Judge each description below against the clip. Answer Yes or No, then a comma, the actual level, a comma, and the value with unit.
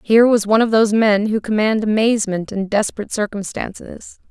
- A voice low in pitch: No, high, 215 Hz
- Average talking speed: Yes, average, 165 wpm